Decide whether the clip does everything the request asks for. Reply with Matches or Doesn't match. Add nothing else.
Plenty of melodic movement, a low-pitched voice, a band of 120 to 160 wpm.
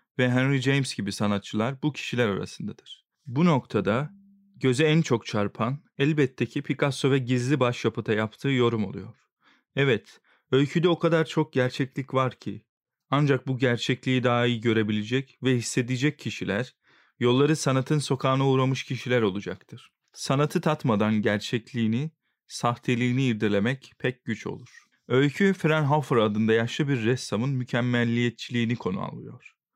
Doesn't match